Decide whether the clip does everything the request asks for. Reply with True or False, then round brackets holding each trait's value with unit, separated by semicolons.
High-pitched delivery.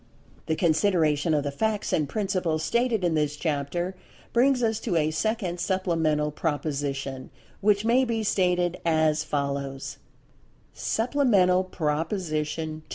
False (165 Hz)